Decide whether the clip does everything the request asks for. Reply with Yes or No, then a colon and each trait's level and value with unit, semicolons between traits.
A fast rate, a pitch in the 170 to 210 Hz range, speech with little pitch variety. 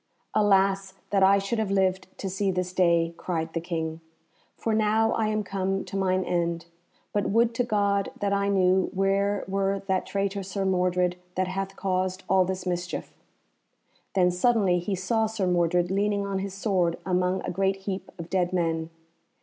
No: average, 175 wpm; high, 190 Hz; narrow, 1.6 semitones